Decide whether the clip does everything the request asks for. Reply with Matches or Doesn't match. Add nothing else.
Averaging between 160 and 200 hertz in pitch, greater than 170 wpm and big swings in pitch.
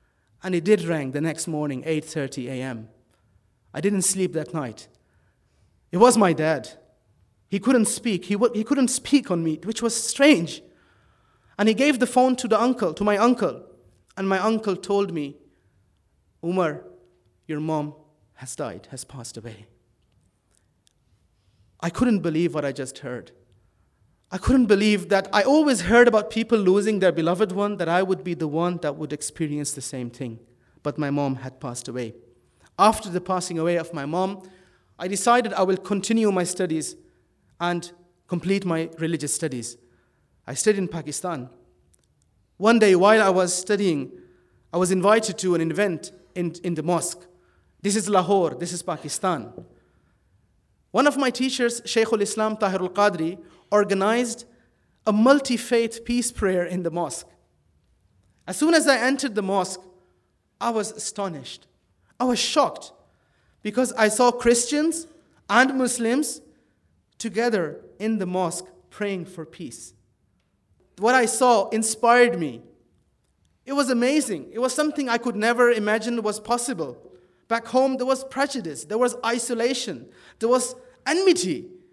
Doesn't match